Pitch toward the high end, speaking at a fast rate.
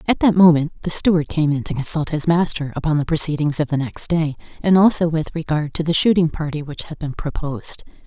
No: medium, 160 Hz; fast, 225 wpm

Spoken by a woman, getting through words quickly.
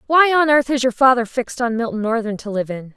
Yes: female; fast, 265 wpm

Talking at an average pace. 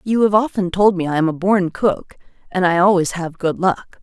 No: fast, 240 wpm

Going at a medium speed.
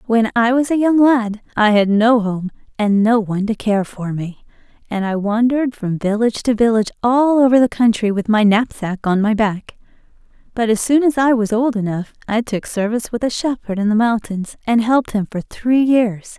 No: fast, 210 wpm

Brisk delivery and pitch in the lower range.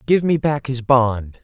Yes: fast, 210 wpm; low, 130 Hz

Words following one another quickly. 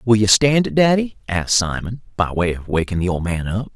Yes: fast, 240 wpm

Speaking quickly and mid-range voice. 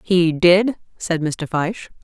No: average, 145 wpm; medium, 175 Hz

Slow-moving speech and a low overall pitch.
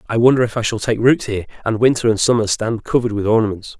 No: fast, 255 wpm; low, 110 Hz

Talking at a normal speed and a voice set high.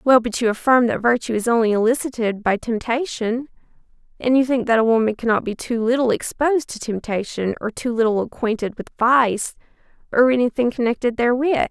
Yes: average, 170 wpm; high, 235 Hz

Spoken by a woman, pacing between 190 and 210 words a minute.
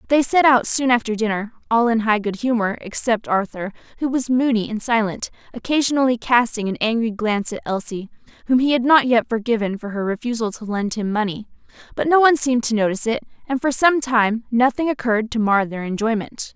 Yes: female; average, 200 wpm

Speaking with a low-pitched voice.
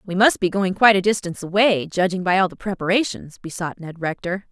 No: high, 190 Hz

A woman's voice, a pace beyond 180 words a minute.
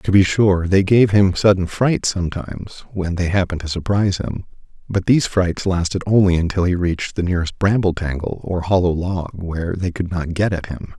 No: male; average, 200 wpm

